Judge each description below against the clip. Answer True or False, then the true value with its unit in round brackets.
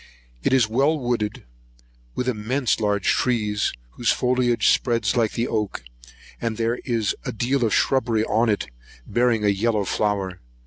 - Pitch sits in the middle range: False (115 Hz)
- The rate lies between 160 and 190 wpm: True (165 wpm)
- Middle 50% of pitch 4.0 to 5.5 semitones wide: False (2.7 semitones)